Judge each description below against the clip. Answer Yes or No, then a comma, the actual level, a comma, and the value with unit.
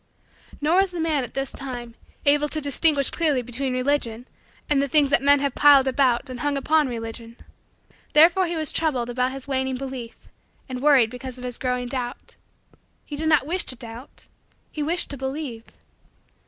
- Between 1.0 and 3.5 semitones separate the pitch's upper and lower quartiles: Yes, average, 2.9 semitones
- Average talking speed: Yes, average, 180 wpm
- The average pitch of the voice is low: No, very high, 270 Hz